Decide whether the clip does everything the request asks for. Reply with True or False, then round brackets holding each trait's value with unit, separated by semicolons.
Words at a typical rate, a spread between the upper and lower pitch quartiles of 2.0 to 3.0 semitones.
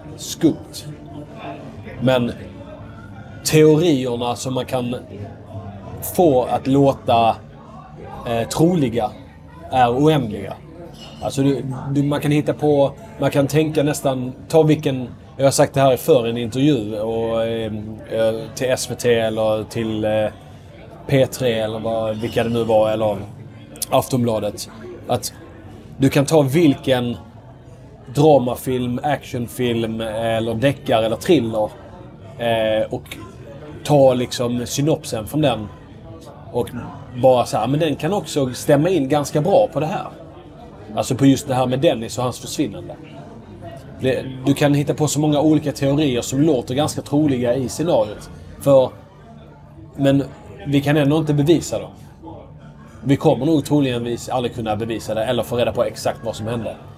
False (140 wpm; 4.0 semitones)